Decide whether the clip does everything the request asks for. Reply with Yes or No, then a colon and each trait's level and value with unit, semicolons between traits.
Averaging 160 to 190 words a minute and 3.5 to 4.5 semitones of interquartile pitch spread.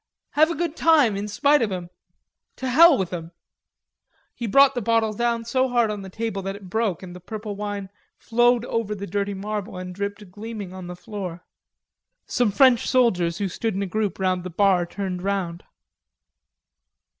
Yes: average, 185 wpm; average, 3.8 semitones